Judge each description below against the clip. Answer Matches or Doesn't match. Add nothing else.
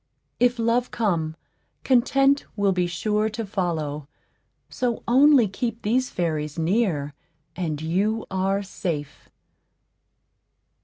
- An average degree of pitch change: Doesn't match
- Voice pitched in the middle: Doesn't match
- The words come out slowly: Matches